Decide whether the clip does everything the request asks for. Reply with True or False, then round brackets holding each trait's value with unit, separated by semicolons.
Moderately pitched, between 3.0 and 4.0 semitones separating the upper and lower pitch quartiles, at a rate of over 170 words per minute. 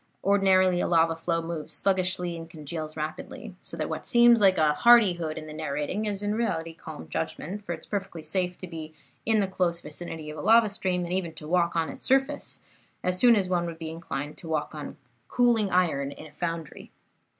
True (170 Hz; 3.4 semitones; 205 wpm)